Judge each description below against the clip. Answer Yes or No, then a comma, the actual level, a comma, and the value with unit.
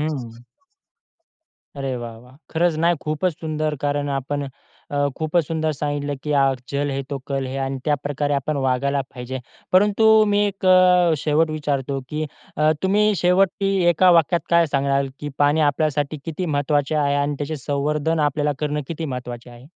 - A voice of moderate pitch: Yes, medium, 145 Hz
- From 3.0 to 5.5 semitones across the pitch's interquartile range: No, narrow, 2.6 semitones